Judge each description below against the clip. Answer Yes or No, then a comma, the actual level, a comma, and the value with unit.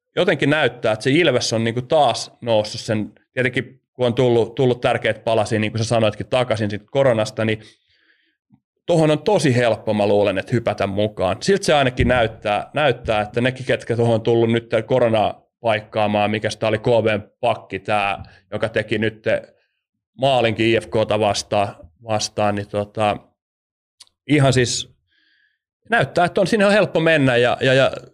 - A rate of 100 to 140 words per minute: No, fast, 155 wpm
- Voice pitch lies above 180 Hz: No, low, 115 Hz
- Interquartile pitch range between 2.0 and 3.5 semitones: Yes, average, 3.2 semitones